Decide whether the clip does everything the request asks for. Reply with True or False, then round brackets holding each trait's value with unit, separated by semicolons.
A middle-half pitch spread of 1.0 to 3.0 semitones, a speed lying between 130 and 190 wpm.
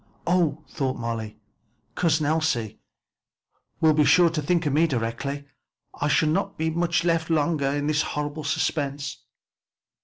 True (2.5 semitones; 150 wpm)